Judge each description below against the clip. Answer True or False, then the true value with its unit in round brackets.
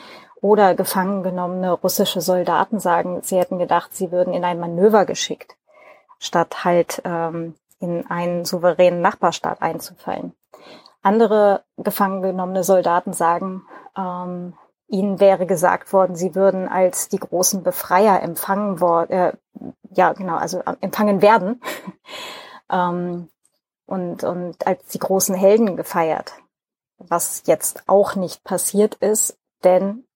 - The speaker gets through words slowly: True (120 wpm)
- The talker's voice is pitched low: False (185 Hz)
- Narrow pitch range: True (1.8 semitones)